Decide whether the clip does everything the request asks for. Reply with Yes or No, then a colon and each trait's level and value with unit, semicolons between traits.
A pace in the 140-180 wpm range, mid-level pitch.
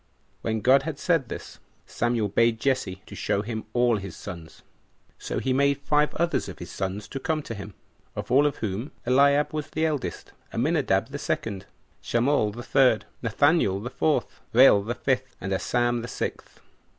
No: average, 175 wpm; low, 120 Hz